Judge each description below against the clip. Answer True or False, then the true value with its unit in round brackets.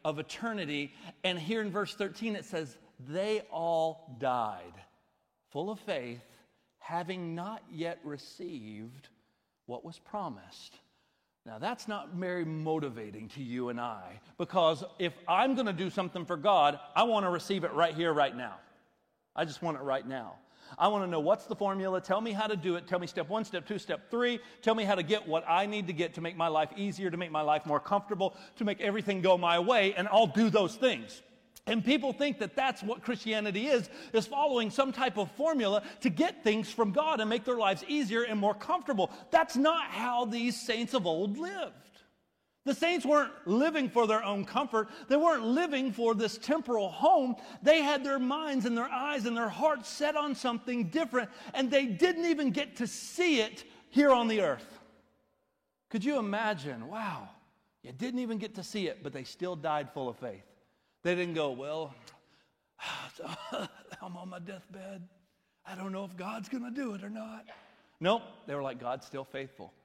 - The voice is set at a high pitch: True (205 Hz)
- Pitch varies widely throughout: True (6.3 semitones)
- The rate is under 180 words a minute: False (195 wpm)